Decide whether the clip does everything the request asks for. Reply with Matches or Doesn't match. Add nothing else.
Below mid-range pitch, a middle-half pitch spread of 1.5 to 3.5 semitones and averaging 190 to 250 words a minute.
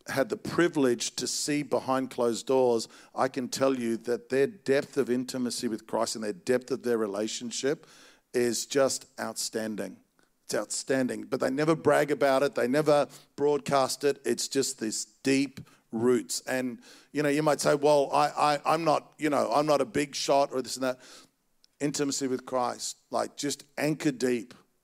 Doesn't match